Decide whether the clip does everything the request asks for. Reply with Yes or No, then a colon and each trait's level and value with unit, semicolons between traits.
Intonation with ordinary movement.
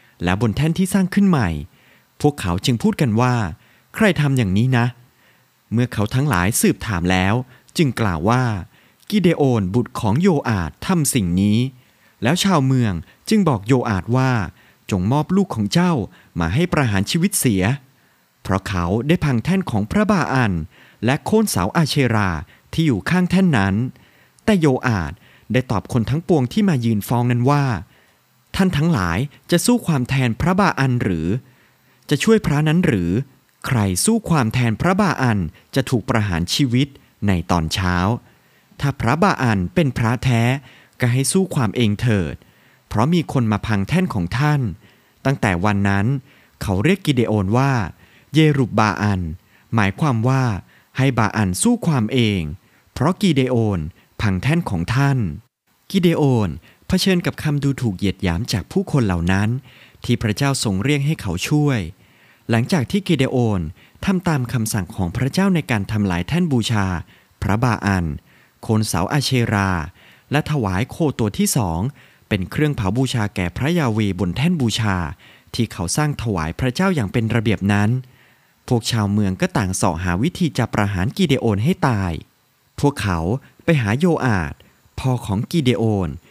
No: wide, 6.2 semitones